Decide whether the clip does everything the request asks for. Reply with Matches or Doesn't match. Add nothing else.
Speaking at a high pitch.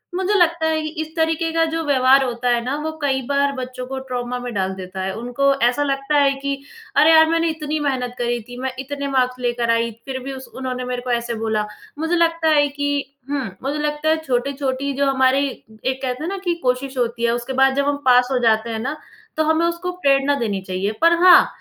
Matches